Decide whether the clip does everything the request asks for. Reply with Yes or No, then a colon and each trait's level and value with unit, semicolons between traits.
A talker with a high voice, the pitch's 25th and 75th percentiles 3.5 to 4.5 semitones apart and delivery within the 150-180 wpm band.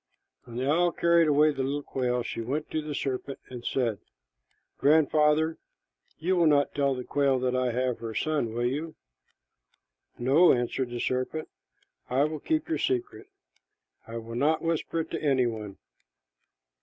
No: medium, 140 Hz; average, 4.0 semitones; average, 165 wpm